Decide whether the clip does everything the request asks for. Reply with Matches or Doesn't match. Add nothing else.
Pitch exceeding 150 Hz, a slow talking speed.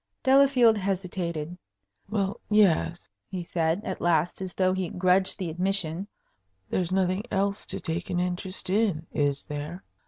Doesn't match